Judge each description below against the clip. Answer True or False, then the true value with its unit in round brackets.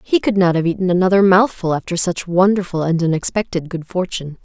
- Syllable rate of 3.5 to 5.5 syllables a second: False (6.0 syllables/s)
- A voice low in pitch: False (180 Hz)